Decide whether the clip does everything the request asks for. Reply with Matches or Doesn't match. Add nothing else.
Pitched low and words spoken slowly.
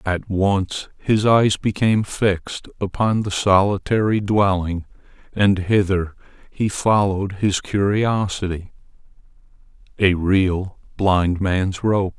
Matches